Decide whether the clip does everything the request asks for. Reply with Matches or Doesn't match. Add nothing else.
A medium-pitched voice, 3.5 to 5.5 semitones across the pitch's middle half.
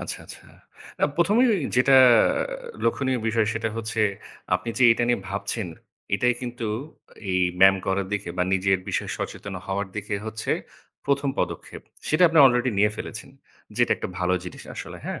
Doesn't match